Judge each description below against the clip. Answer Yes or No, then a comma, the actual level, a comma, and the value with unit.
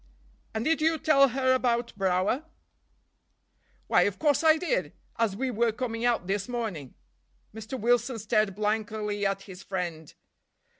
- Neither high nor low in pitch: No, high, 225 Hz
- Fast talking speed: No, average, 140 wpm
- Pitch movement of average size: Yes, average, 4.4 semitones